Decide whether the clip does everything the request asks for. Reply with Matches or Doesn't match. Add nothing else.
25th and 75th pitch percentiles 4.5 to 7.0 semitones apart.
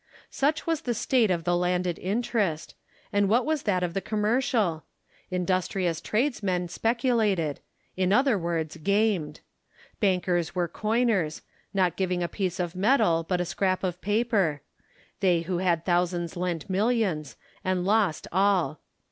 Doesn't match